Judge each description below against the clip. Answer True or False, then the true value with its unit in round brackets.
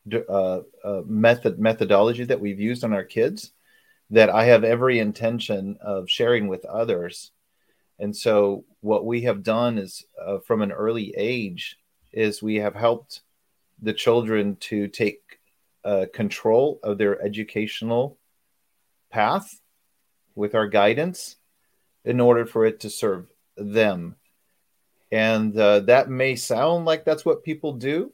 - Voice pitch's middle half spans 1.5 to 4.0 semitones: True (2.7 semitones)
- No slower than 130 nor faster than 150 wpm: True (140 wpm)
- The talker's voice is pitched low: True (110 Hz)